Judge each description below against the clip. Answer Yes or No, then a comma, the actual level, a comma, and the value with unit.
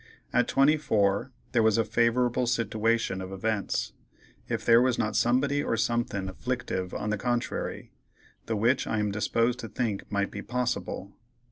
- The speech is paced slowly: No, average, 155 wpm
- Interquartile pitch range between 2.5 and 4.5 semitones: Yes, average, 3.0 semitones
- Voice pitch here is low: Yes, low, 115 Hz